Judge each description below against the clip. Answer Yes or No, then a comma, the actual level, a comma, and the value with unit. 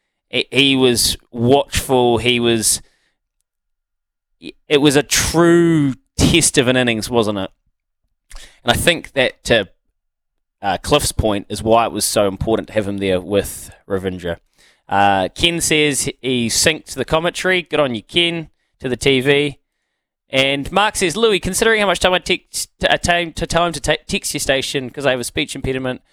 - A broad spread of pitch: Yes, wide, 6.3 semitones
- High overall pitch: No, low, 135 Hz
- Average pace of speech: Yes, average, 170 wpm